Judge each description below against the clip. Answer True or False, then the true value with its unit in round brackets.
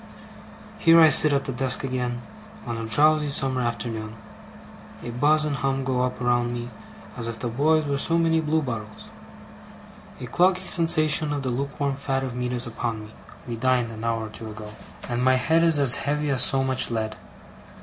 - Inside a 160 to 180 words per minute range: False (190 wpm)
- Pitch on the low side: True (130 Hz)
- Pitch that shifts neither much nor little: True (3.6 semitones)